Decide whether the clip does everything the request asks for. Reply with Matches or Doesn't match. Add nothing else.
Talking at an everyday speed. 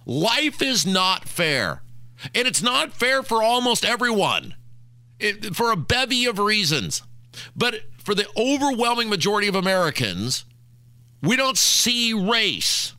Doesn't match